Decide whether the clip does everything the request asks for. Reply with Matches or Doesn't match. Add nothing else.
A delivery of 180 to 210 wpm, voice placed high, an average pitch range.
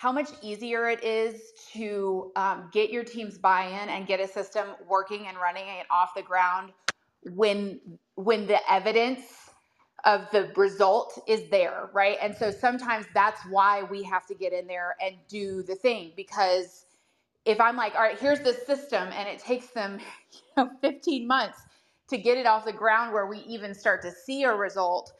Matches